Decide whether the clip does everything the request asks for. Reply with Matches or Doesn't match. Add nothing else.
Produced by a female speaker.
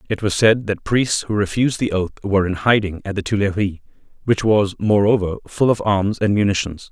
Doesn't match